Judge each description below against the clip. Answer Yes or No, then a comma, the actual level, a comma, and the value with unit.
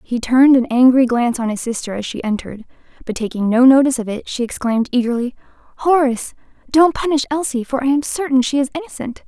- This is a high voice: Yes, very high, 255 Hz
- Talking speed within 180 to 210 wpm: Yes, average, 200 wpm